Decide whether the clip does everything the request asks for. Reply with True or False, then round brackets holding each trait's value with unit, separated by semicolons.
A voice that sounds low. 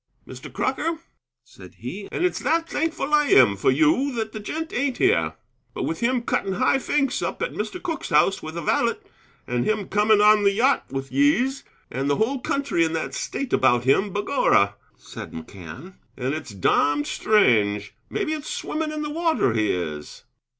False (210 Hz)